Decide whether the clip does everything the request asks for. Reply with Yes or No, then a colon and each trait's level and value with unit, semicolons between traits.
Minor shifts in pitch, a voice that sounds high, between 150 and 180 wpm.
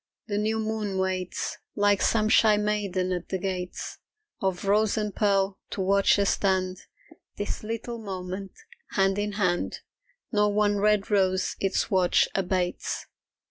No: narrow, 1.9 semitones; high, 200 Hz; average, 140 wpm